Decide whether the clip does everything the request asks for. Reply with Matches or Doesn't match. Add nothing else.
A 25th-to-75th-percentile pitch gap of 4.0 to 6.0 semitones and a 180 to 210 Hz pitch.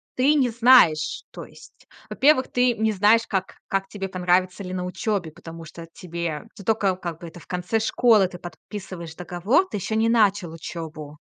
Matches